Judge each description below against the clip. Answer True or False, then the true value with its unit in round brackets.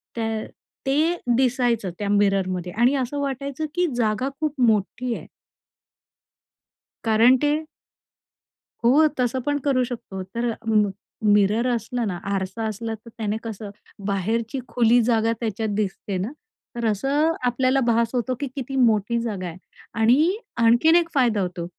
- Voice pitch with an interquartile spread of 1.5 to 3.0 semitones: False (3.7 semitones)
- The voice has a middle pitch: False (235 Hz)